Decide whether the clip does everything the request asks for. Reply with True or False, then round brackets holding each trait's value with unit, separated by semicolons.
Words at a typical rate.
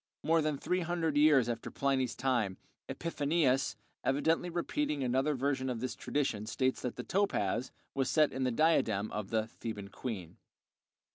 True (155 wpm)